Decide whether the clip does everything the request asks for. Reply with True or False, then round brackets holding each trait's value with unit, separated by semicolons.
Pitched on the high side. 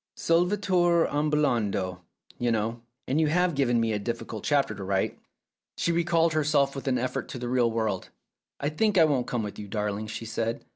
False (125 Hz)